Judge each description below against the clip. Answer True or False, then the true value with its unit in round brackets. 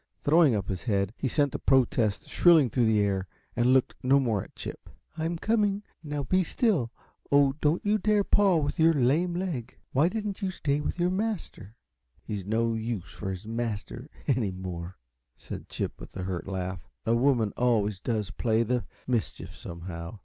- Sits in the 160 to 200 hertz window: False (125 Hz)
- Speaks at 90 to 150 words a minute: False (180 wpm)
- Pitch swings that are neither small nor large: False (7.8 semitones)